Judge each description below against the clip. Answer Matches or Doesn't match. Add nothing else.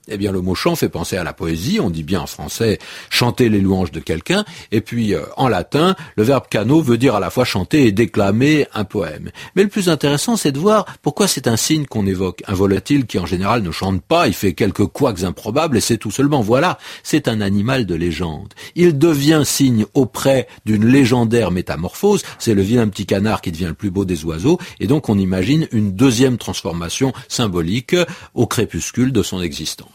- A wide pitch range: Matches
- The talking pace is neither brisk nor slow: Matches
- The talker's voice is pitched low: Matches